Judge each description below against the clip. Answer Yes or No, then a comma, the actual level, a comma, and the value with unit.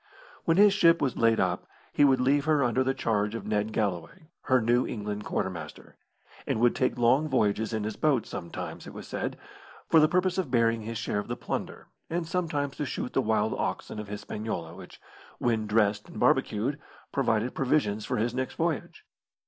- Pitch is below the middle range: Yes, low, 120 Hz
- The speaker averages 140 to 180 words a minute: No, average, 190 wpm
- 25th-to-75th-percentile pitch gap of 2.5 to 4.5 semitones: No, average, 5.2 semitones